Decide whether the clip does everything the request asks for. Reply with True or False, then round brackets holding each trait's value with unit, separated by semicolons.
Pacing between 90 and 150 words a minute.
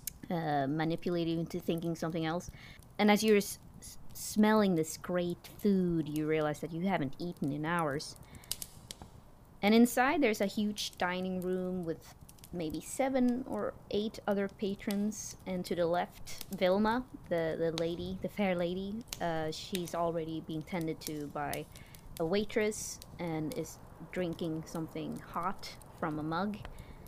True (140 wpm)